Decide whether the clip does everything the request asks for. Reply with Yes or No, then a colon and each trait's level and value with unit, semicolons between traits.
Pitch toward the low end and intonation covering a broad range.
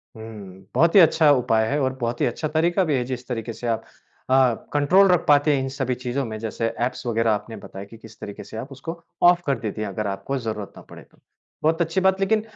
Yes: low, 130 Hz; wide, 5.7 semitones